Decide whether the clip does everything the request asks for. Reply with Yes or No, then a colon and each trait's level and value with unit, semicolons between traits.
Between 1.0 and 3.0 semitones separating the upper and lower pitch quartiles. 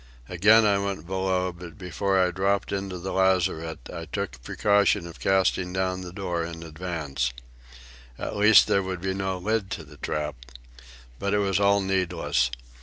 Yes: narrow, 2.4 semitones